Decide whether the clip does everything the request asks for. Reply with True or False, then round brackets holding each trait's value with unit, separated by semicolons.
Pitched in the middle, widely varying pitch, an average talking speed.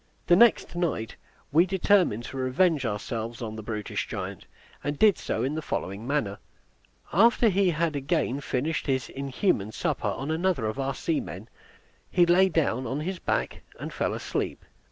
True (145 Hz; 6.6 semitones; 165 wpm)